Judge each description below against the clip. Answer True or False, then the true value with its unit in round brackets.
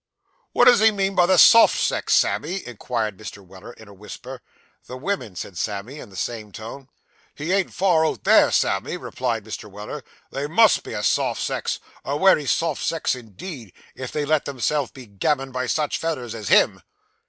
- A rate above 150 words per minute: True (190 wpm)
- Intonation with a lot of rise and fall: True (7.0 semitones)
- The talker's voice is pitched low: True (130 Hz)